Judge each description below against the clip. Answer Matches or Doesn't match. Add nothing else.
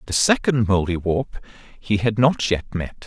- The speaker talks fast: Doesn't match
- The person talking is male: Matches